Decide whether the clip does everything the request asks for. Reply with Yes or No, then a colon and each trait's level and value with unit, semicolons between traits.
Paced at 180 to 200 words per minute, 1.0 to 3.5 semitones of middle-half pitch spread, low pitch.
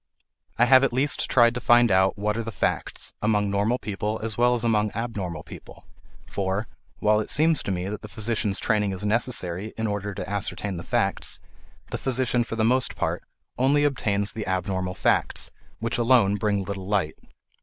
Yes: average, 185 wpm; average, 3.1 semitones; low, 105 Hz